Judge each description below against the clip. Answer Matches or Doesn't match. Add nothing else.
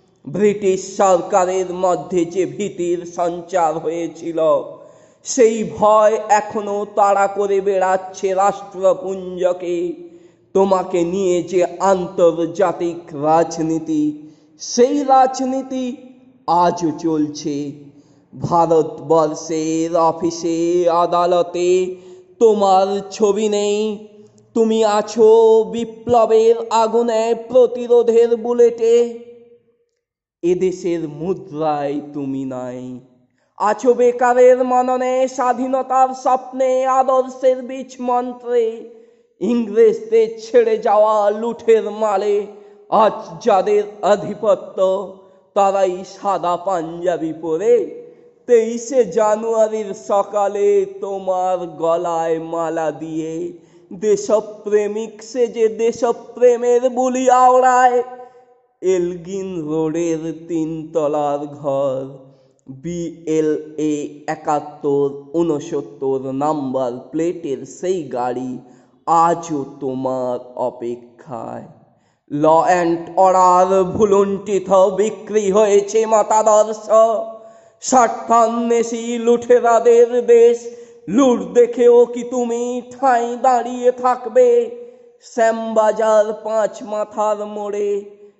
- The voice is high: Matches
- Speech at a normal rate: Matches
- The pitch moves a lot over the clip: Matches